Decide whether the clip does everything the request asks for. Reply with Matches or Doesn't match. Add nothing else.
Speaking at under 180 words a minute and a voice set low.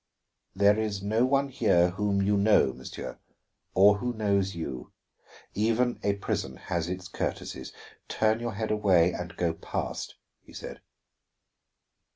Matches